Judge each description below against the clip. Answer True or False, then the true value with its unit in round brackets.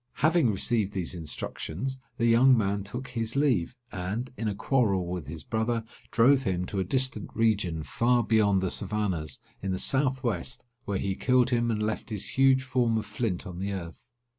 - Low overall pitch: True (110 Hz)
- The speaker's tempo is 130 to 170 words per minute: False (190 wpm)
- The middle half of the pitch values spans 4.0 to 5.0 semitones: True (4.7 semitones)